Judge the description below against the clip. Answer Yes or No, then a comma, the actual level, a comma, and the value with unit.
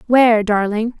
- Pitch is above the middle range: Yes, high, 220 Hz